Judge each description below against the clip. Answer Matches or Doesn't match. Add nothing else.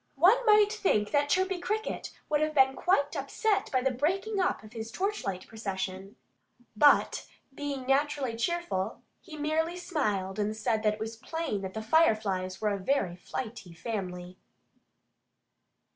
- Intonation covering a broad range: Matches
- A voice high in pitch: Matches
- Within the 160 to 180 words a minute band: Doesn't match